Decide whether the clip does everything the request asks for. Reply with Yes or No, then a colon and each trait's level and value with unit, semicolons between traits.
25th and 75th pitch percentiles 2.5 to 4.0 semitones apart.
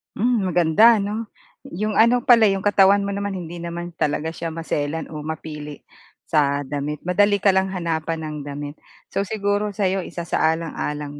No: average, 4.5 semitones